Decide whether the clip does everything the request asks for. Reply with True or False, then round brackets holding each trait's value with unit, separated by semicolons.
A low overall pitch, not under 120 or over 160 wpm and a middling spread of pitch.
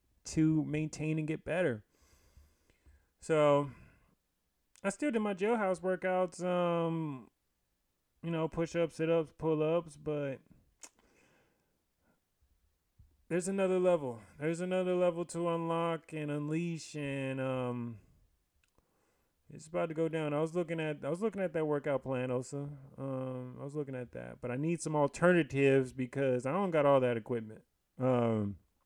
False (150 Hz; 145 wpm; 4.9 semitones)